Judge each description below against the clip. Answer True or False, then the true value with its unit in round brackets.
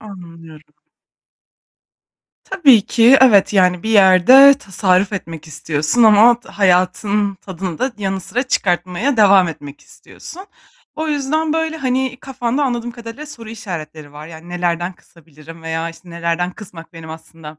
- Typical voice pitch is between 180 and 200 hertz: True (190 Hz)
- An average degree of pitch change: False (6.3 semitones)